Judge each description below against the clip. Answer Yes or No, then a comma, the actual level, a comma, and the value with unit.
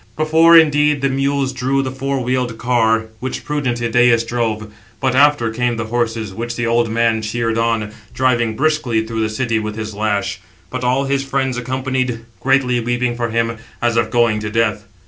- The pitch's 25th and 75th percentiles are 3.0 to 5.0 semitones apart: No, narrow, 2.6 semitones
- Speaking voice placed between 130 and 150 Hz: No, low, 120 Hz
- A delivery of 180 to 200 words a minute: Yes, average, 185 wpm